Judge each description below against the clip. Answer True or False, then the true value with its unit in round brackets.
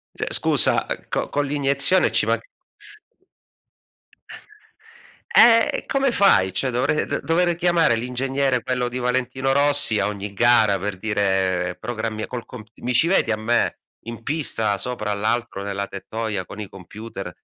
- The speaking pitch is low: True (120 Hz)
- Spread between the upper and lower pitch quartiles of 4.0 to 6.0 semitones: True (4.9 semitones)